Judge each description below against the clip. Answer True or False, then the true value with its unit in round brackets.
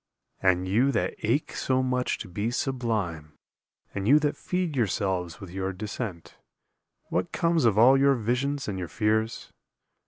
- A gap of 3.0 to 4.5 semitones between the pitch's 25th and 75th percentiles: False (5.6 semitones)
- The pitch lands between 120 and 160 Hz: False (110 Hz)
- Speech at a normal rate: True (155 wpm)